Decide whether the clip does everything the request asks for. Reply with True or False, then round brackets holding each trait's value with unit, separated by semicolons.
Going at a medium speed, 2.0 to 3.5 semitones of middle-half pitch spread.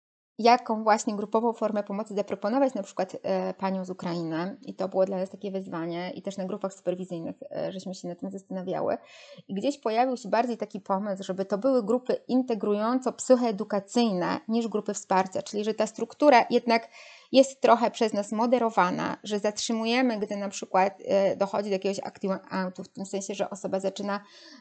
False (175 wpm; 3.2 semitones)